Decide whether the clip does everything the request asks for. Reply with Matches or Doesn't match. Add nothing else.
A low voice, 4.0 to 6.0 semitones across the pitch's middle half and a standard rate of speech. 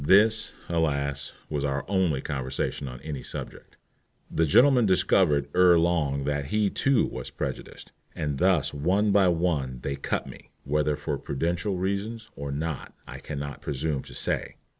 Matches